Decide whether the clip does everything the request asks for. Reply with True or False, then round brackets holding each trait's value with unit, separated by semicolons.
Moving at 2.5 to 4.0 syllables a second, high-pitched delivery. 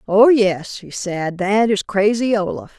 True (3.9 syllables/s; 205 Hz)